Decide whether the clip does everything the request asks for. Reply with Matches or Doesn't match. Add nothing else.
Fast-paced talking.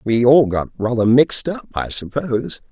Doesn't match